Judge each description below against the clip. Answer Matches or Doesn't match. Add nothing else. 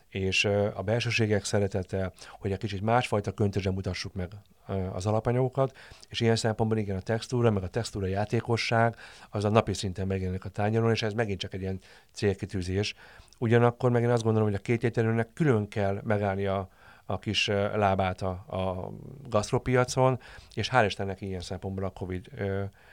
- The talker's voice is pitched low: Matches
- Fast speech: Matches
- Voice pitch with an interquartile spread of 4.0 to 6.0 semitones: Doesn't match